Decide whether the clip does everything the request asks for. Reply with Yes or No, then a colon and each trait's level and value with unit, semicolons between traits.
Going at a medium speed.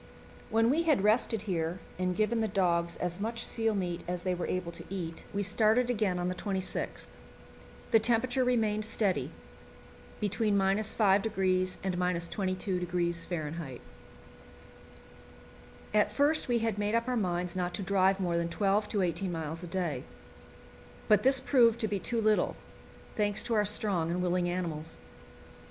Yes: average, 155 wpm